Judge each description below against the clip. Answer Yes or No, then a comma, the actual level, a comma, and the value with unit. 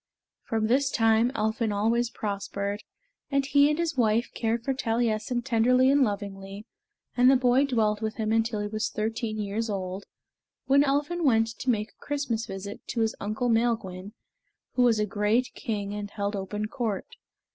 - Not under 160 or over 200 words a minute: Yes, average, 170 wpm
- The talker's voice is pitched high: Yes, high, 225 Hz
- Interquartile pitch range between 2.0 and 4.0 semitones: Yes, average, 3.1 semitones